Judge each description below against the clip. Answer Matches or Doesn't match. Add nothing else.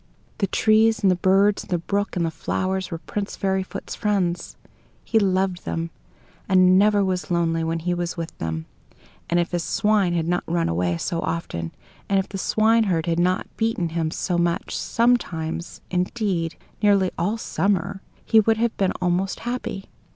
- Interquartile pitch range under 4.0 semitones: Matches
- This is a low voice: Doesn't match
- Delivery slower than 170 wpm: Doesn't match